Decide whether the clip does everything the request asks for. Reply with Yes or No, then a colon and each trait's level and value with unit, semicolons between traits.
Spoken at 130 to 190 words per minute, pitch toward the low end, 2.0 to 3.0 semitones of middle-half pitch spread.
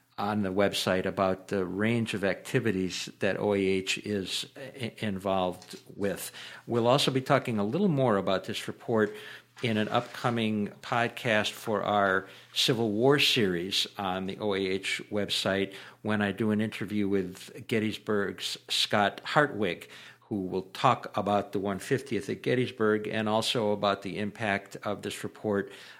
Yes: average, 140 wpm; low, 105 Hz; average, 2.7 semitones